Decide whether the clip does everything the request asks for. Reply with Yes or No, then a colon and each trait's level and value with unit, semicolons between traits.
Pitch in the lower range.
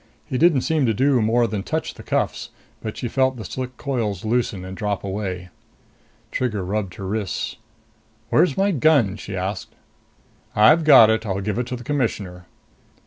Yes: low, 110 Hz